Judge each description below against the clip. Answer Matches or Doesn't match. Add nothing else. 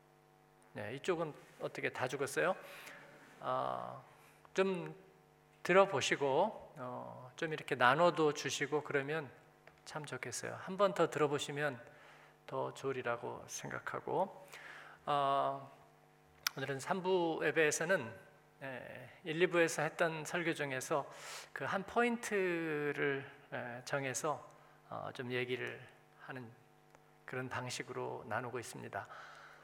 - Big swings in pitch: Doesn't match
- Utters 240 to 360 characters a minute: Doesn't match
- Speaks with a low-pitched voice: Doesn't match